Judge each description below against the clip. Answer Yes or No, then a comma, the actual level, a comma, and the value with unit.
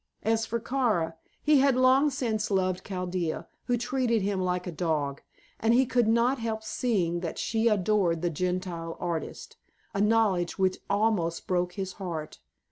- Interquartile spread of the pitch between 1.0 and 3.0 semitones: No, average, 4.6 semitones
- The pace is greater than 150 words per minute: Yes, average, 160 wpm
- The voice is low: No, high, 200 Hz